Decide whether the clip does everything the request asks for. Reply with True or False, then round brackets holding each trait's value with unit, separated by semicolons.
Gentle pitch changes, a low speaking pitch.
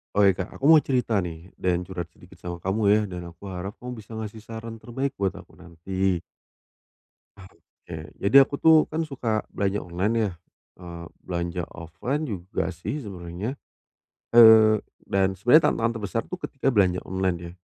False (4.5 semitones; 100 Hz)